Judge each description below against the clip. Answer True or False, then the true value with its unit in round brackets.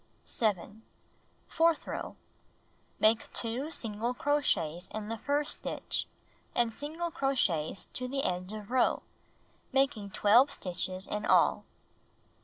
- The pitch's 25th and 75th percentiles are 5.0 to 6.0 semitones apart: True (5.4 semitones)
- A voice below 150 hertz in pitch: False (225 Hz)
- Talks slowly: True (115 wpm)